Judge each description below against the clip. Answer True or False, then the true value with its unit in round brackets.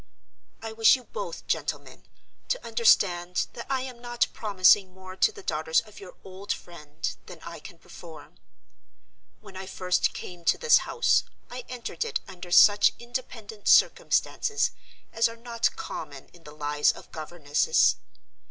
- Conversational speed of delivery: True (150 wpm)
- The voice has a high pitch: True (205 Hz)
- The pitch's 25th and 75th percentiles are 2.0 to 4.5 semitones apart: False (5.2 semitones)